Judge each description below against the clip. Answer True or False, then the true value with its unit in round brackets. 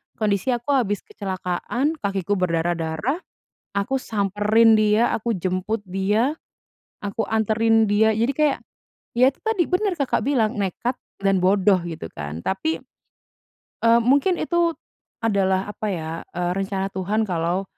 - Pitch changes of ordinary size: True (3.9 semitones)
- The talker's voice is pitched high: True (210 Hz)